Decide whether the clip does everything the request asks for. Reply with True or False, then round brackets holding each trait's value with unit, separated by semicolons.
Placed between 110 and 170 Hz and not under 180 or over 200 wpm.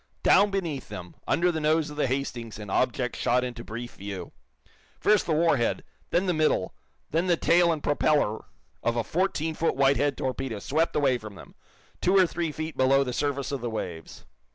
True (140 Hz; 195 wpm)